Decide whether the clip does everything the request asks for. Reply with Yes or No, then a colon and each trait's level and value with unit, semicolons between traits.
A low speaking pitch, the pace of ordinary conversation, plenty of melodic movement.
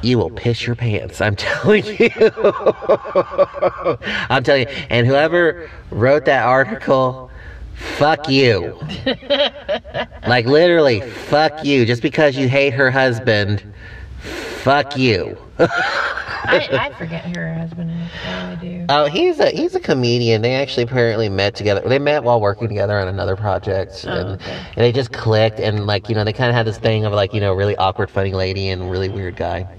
Yes: low, 120 Hz; average, 160 wpm; wide, 6.5 semitones